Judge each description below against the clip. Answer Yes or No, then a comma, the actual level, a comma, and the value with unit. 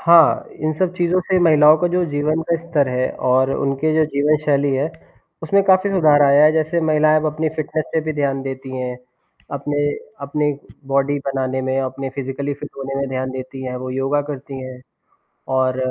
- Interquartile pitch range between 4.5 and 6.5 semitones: No, average, 2.8 semitones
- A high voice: No, medium, 145 Hz